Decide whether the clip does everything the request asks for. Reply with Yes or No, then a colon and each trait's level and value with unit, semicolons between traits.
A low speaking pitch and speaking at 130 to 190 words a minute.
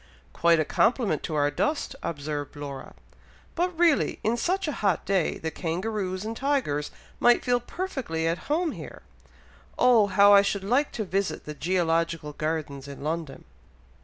No: medium, 185 Hz; average, 160 wpm